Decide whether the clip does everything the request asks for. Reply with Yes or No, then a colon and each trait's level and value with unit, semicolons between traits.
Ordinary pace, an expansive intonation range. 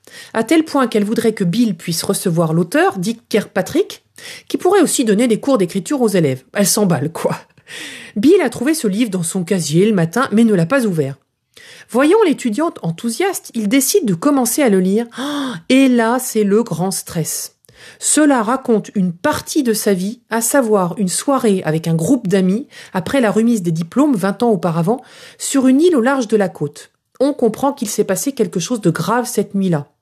Yes: average, 195 wpm; wide, 6.1 semitones